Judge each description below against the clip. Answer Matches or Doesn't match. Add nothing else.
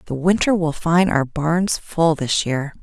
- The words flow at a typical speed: Matches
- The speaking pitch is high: Doesn't match